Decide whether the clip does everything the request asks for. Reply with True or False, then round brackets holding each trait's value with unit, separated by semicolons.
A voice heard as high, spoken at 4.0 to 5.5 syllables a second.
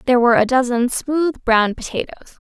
False (250 Hz; 6.0 syllables/s)